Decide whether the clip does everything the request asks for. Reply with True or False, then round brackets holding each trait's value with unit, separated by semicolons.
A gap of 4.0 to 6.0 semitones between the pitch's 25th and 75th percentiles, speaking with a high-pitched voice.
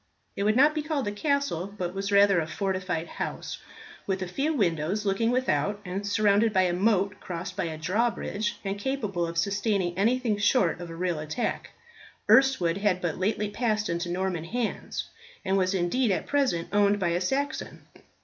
False (3.6 semitones; 200 Hz)